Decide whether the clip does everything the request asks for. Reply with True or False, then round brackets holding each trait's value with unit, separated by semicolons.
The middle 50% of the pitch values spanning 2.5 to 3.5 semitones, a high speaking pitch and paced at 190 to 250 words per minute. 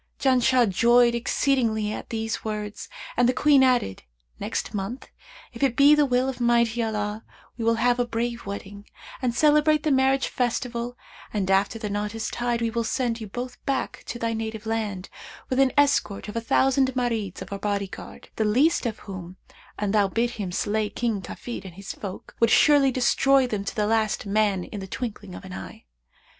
True (3.2 semitones; 230 Hz; 195 wpm)